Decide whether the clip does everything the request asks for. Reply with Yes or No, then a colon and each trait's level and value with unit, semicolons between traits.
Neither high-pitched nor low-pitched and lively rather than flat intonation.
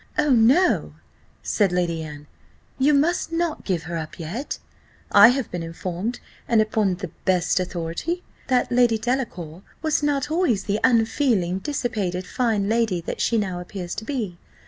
No: high, 215 Hz; wide, 6.5 semitones